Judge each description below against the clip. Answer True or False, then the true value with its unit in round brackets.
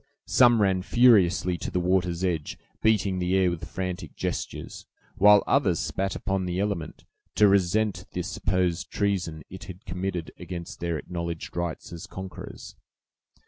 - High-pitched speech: False (90 Hz)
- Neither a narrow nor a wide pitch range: False (2.1 semitones)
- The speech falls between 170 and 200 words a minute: False (145 wpm)